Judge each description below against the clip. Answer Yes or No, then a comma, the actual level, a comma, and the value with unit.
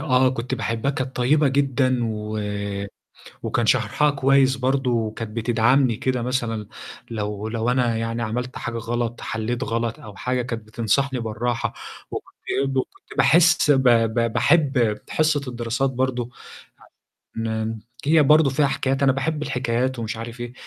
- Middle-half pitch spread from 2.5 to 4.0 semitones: Yes, average, 2.8 semitones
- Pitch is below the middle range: Yes, low, 120 Hz